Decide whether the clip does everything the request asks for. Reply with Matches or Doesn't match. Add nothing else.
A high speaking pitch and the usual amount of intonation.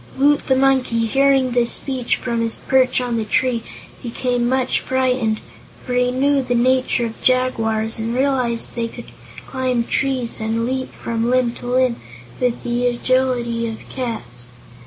Doesn't match